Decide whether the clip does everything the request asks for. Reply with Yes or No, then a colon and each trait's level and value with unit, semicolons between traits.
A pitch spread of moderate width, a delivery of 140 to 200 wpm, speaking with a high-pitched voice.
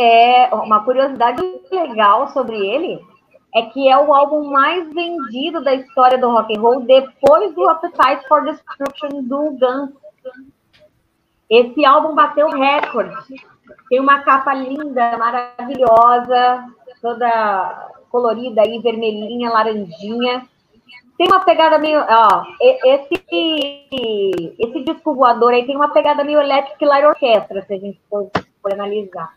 No: average, 4.2 semitones; average, 130 wpm; very high, 260 Hz